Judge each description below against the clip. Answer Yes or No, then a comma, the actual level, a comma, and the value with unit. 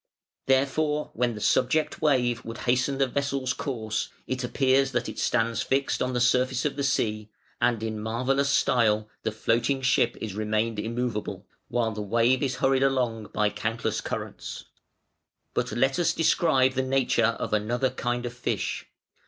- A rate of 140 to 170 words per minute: Yes, average, 160 wpm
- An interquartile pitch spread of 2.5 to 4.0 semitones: Yes, average, 3.0 semitones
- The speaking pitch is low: Yes, low, 125 Hz